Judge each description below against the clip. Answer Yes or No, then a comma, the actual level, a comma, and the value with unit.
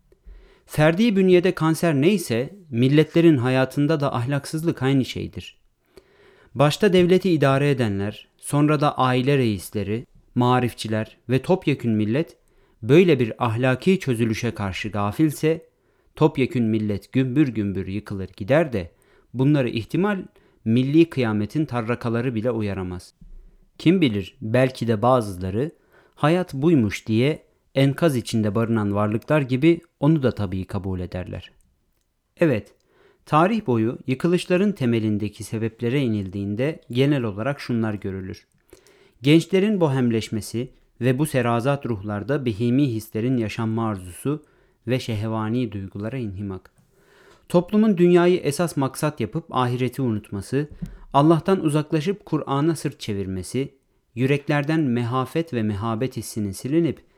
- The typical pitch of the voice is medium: No, low, 130 Hz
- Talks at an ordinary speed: Yes, average, 110 wpm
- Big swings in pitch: Yes, wide, 5.7 semitones